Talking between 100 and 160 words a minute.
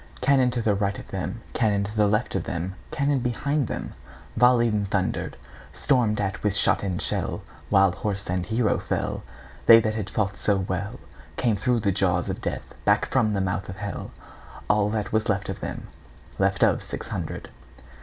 Yes: average, 150 wpm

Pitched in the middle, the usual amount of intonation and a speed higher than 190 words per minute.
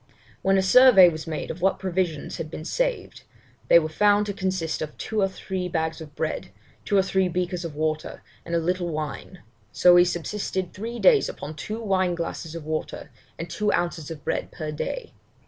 Yes: medium, 180 Hz; average, 3.2 semitones; average, 200 wpm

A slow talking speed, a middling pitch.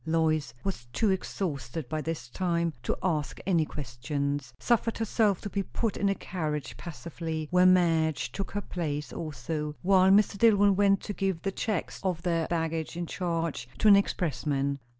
No: average, 170 wpm; medium, 165 Hz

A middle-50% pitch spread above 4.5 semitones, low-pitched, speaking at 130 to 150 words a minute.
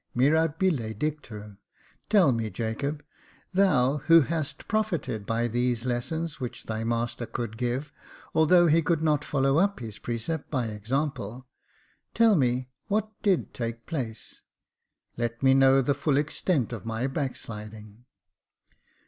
Yes: average, 5.1 semitones; low, 130 Hz; average, 140 wpm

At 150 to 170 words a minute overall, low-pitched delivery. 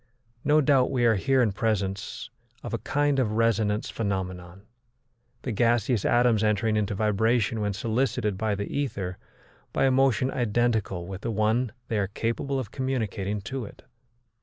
Yes: average, 160 wpm; low, 110 Hz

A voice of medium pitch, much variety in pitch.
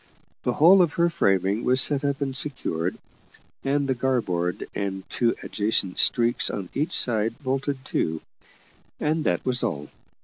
No: low, 125 Hz; wide, 6.3 semitones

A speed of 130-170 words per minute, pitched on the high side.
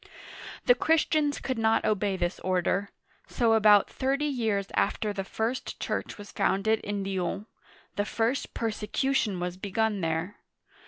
Yes: average, 140 wpm; high, 210 Hz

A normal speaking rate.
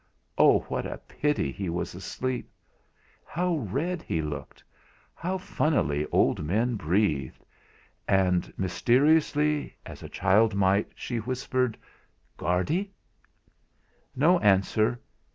No: slow, 105 wpm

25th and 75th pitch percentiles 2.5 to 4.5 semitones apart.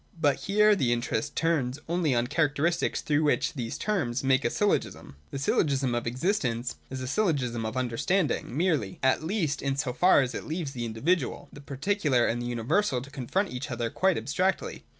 No: wide, 5.5 semitones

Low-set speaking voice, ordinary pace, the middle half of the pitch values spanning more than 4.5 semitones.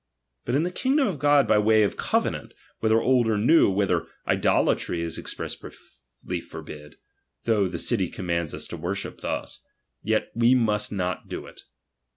Yes: low, 105 Hz; average, 165 wpm; wide, 5.6 semitones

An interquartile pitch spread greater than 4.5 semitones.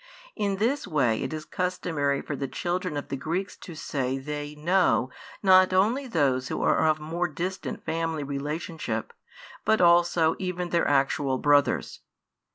No: average, 4.1 semitones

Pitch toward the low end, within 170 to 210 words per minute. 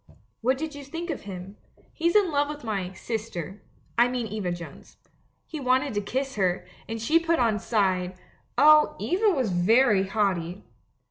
No: high, 230 Hz; average, 180 wpm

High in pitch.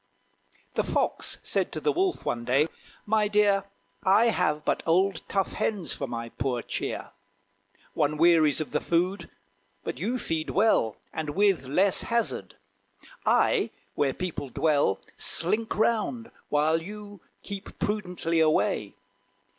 No: medium, 180 Hz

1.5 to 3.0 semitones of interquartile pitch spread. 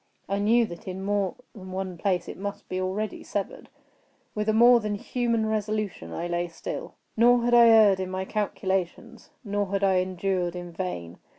Yes: average, 2.7 semitones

